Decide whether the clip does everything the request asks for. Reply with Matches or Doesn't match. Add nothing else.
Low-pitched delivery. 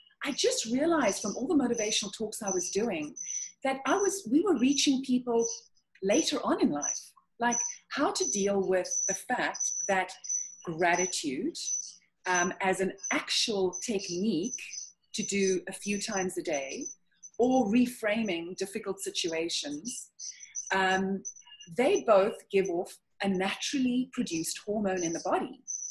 Doesn't match